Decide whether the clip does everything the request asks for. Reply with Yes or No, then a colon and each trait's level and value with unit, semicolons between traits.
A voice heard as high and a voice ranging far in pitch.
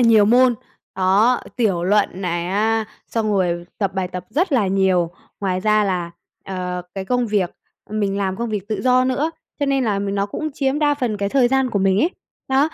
No: high, 210 Hz; average, 4.7 semitones